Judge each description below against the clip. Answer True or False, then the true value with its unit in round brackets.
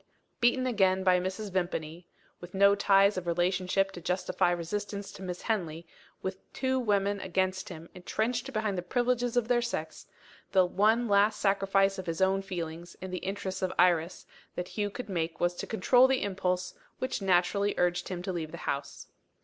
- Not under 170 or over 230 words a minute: True (180 wpm)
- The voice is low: False (190 Hz)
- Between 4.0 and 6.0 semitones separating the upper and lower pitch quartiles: False (2.5 semitones)